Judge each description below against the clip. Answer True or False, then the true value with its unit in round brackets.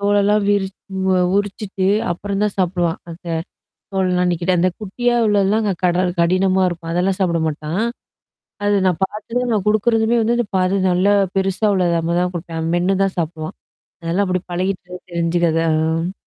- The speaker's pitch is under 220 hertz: True (185 Hz)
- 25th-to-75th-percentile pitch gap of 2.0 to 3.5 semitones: True (2.8 semitones)